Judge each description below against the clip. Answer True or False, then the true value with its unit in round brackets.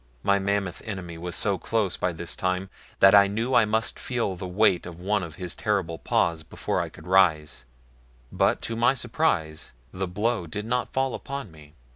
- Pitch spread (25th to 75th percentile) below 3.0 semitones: False (4.2 semitones)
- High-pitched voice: False (95 Hz)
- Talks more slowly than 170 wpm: False (190 wpm)